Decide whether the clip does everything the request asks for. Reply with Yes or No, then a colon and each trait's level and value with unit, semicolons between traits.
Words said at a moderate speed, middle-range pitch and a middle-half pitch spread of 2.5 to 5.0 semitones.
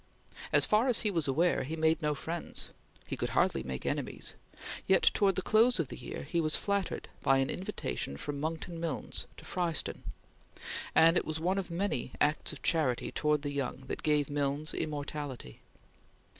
Yes: average, 180 wpm; medium, 155 Hz; average, 3.6 semitones